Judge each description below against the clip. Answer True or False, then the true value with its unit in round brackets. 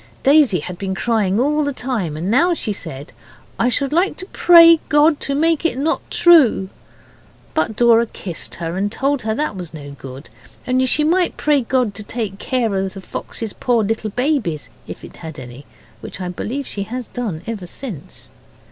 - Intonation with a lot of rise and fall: True (7.0 semitones)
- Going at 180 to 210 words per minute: True (190 wpm)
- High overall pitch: True (230 Hz)